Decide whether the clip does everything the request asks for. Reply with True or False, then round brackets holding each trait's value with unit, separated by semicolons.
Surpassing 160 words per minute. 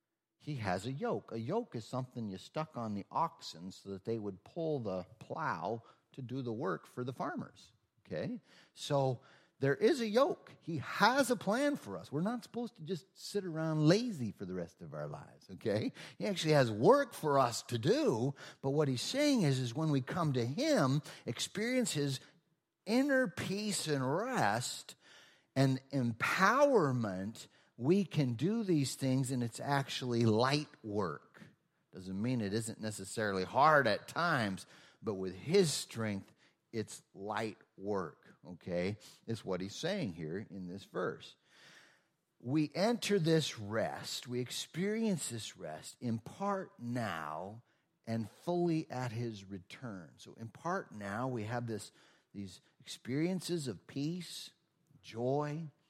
False (155 wpm)